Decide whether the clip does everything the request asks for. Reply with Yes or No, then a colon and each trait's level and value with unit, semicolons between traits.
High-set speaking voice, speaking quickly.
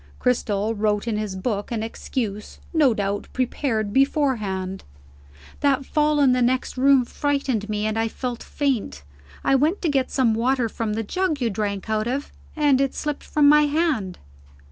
No: high, 245 Hz; average, 170 wpm